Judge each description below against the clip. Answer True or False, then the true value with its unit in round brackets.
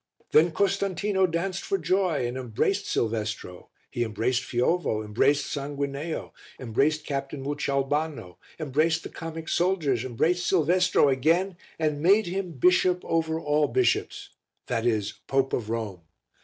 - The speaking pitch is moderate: True (145 Hz)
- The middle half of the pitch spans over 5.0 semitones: True (5.6 semitones)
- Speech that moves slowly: True (130 wpm)